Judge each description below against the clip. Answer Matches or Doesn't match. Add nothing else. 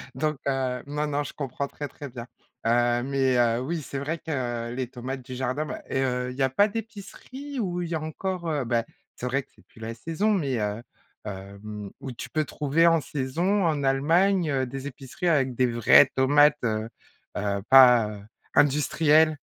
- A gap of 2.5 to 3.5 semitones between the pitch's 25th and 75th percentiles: Doesn't match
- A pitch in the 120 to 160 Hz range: Matches